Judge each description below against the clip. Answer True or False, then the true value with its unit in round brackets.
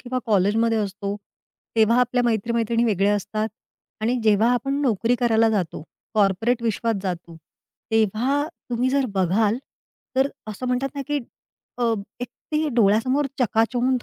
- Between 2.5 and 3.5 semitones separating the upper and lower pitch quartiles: True (3.1 semitones)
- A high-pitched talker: True (230 Hz)